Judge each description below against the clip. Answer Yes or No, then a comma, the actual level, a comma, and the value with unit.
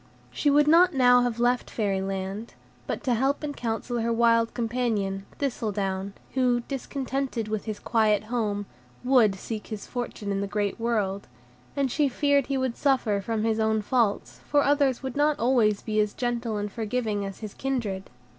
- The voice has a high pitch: Yes, high, 230 Hz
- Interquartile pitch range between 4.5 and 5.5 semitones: No, average, 3.8 semitones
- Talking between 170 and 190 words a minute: Yes, average, 175 wpm